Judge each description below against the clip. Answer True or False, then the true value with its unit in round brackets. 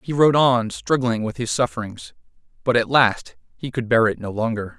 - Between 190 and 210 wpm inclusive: True (200 wpm)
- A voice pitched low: True (120 Hz)